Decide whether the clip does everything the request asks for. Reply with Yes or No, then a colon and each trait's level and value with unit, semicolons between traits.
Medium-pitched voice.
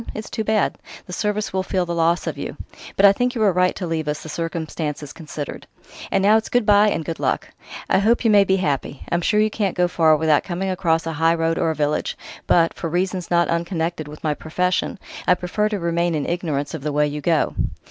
Yes: medium, 170 Hz